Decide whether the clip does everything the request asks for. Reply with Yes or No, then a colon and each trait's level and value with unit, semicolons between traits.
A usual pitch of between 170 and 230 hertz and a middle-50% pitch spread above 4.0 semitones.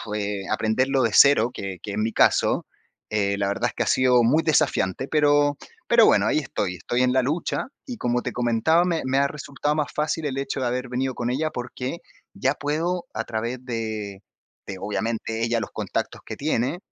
No: low, 125 Hz; average, 4.5 semitones